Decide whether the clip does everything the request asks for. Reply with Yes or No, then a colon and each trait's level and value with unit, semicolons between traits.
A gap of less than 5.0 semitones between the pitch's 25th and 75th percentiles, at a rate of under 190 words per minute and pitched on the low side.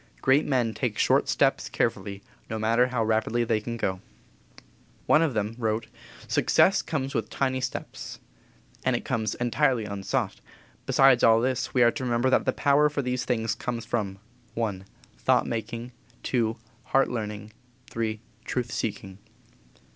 Yes: average, 2.9 semitones; average, 155 wpm; low, 115 Hz